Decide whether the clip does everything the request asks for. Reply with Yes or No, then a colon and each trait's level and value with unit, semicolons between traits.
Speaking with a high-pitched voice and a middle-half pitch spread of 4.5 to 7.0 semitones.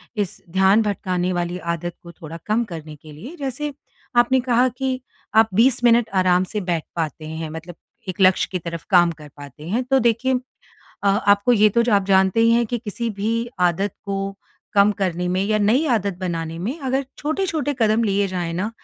Yes: high, 200 Hz; average, 5.0 semitones